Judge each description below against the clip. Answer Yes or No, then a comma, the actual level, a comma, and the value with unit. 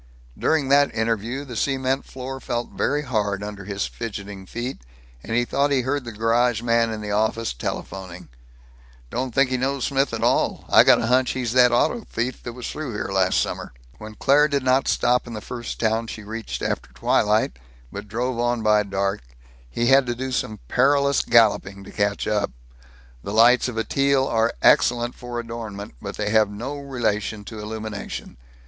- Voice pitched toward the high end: No, low, 115 Hz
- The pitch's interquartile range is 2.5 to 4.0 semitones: Yes, average, 3.4 semitones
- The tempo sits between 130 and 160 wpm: No, average, 190 wpm